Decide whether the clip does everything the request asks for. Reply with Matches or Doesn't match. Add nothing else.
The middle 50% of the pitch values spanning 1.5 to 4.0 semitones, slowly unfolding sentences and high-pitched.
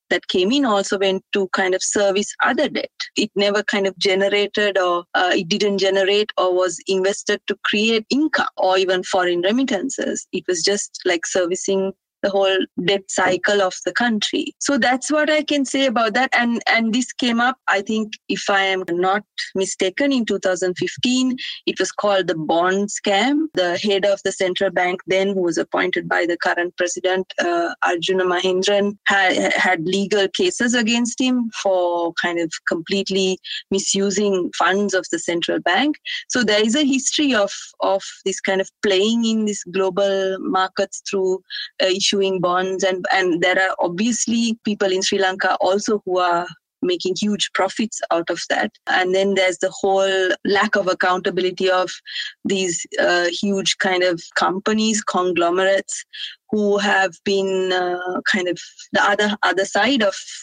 Doesn't match